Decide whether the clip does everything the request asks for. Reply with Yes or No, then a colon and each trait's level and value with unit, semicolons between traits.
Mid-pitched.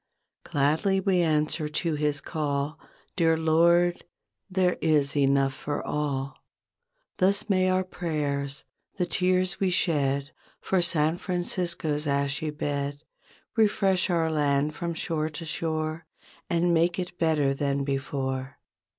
Yes: medium, 155 Hz